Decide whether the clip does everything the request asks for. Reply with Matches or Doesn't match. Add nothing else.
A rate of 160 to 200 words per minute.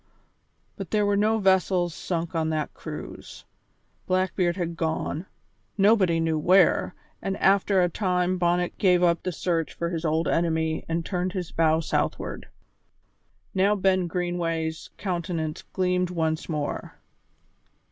Doesn't match